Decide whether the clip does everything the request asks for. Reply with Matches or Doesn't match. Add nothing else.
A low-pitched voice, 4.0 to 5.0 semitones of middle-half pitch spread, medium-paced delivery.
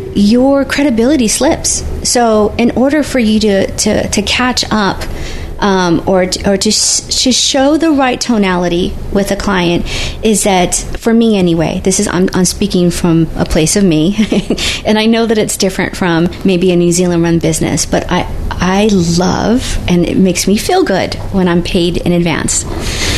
Doesn't match